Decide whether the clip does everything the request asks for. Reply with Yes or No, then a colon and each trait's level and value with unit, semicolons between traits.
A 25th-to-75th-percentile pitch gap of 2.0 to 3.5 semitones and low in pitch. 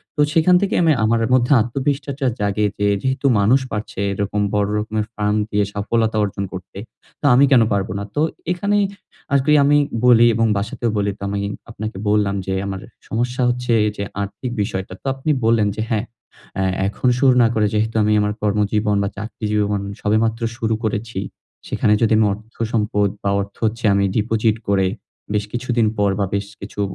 Yes: average, 2.9 semitones; low, 110 Hz